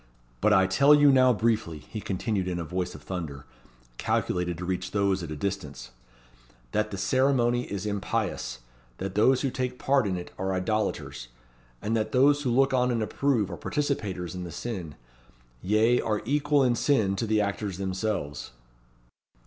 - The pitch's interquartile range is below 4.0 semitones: No, average, 5.2 semitones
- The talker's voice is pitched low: Yes, low, 105 Hz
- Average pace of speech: Yes, average, 175 wpm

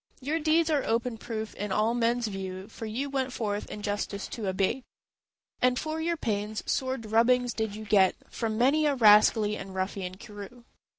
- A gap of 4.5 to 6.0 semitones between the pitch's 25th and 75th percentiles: No, average, 3.5 semitones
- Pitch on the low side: No, high, 225 Hz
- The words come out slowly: No, average, 175 wpm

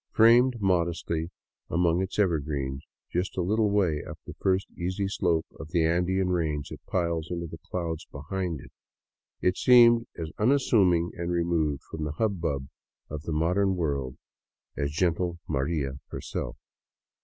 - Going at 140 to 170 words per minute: Yes, average, 155 wpm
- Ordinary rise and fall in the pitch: Yes, average, 3.3 semitones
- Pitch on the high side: No, very low, 85 Hz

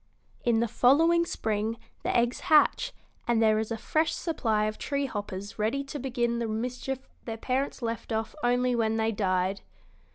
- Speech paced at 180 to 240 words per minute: No, average, 170 wpm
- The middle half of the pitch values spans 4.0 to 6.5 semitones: No, average, 3.3 semitones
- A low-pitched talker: No, high, 235 Hz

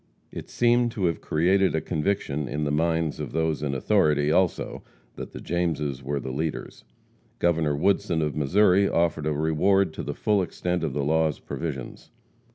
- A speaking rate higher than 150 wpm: Yes, average, 170 wpm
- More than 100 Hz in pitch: No, very low, 80 Hz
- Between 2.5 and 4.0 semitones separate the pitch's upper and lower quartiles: Yes, average, 3.3 semitones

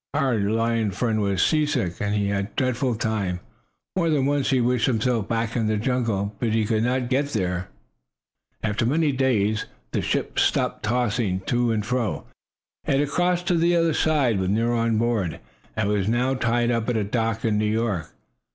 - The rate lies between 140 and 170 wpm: No, average, 190 wpm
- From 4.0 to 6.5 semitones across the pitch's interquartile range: No, average, 3.4 semitones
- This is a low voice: Yes, low, 115 Hz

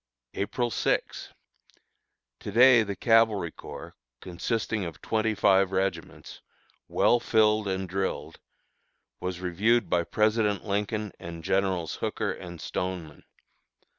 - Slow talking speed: Yes, slow, 110 wpm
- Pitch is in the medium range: No, low, 100 Hz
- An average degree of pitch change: Yes, average, 3.2 semitones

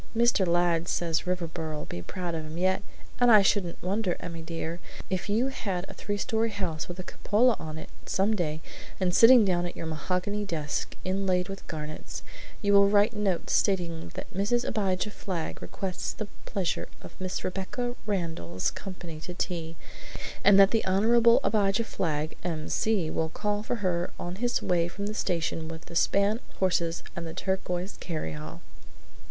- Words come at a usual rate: Yes, average, 170 wpm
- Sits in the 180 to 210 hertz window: Yes, medium, 185 Hz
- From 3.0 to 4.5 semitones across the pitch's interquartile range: Yes, average, 3.5 semitones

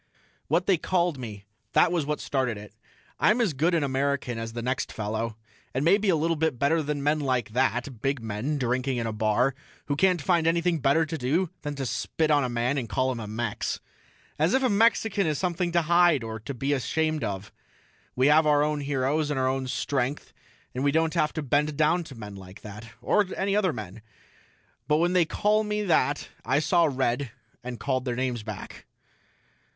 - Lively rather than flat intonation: No, average, 4.9 semitones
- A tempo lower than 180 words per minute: No, fast, 205 wpm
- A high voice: No, medium, 140 Hz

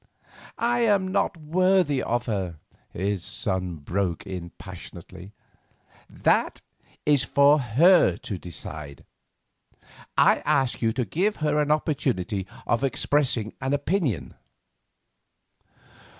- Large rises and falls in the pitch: Yes, wide, 8.4 semitones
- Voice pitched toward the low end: Yes, low, 125 Hz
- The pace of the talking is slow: Yes, slow, 105 wpm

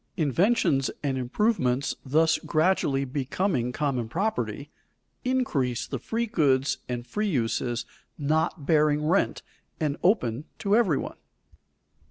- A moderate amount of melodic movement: No, wide, 6.6 semitones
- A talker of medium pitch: Yes, medium, 150 Hz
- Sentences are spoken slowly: Yes, slow, 115 wpm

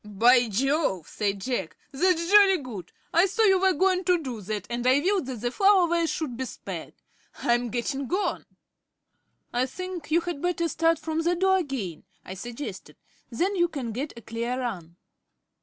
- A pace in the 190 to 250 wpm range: No, average, 180 wpm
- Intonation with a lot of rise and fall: Yes, wide, 6.8 semitones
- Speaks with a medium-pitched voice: No, very high, 275 Hz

